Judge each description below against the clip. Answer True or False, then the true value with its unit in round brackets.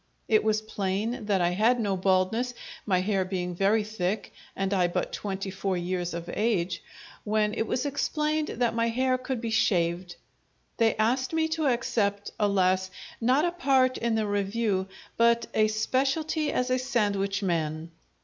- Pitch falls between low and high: False (215 Hz)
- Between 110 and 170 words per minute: True (165 wpm)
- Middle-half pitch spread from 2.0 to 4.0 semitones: False (4.6 semitones)